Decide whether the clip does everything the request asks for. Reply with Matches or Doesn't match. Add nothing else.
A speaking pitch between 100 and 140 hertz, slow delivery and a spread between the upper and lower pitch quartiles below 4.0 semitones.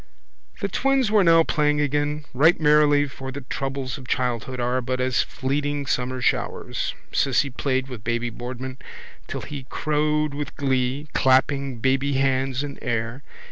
Doesn't match